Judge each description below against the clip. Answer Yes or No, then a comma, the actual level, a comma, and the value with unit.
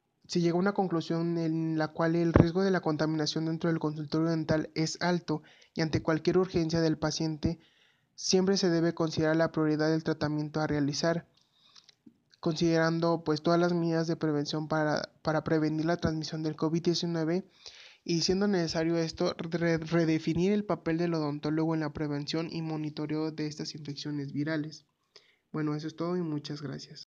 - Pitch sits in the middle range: Yes, medium, 160 Hz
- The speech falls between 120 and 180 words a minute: Yes, average, 165 wpm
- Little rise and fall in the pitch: Yes, narrow, 1.5 semitones